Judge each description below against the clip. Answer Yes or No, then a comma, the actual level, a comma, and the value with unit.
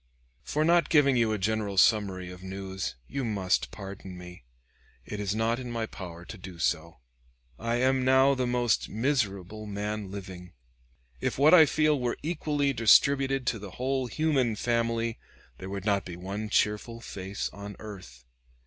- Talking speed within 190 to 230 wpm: No, average, 165 wpm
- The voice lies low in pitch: Yes, low, 110 Hz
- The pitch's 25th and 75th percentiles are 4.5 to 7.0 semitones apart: Yes, average, 4.9 semitones